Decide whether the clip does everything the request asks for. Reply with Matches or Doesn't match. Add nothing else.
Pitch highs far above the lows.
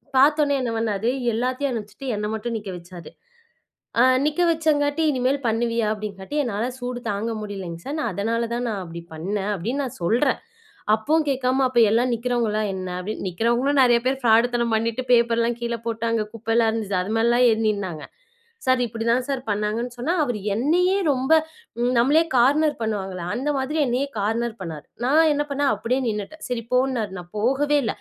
Doesn't match